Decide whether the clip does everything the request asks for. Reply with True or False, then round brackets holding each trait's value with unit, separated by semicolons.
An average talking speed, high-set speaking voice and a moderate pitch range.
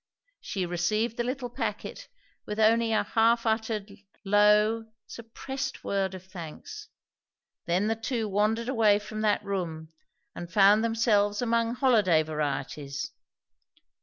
False (125 wpm; 215 Hz; 3.1 semitones)